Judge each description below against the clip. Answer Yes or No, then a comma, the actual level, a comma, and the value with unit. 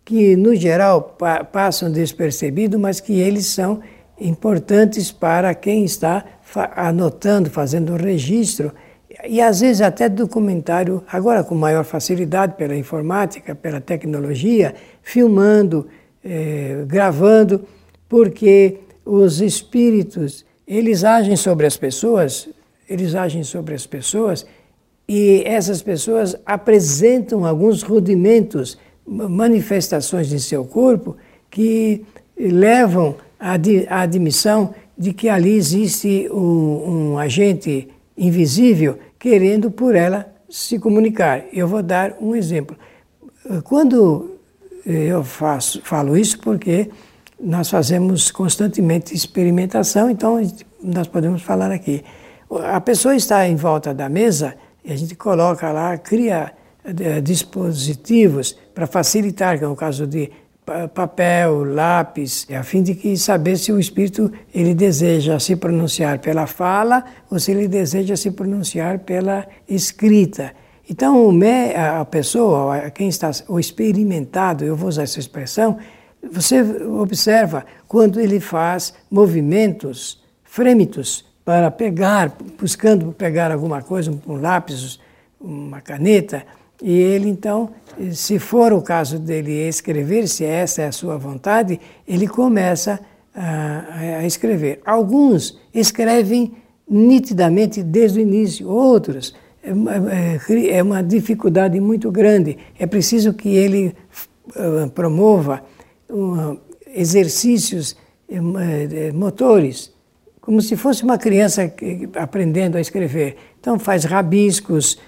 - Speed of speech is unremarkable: No, slow, 115 wpm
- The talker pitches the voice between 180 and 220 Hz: Yes, medium, 185 Hz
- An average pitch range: Yes, average, 4.6 semitones